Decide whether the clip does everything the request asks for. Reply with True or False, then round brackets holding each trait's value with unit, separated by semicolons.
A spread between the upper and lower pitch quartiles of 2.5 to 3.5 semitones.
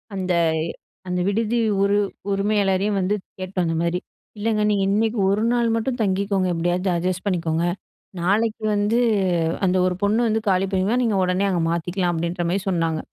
True (2.9 semitones)